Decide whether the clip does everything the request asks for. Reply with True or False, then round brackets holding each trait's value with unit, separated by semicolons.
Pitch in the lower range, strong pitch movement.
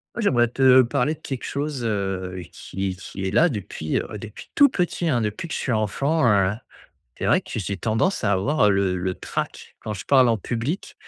True (115 Hz; 6.0 semitones)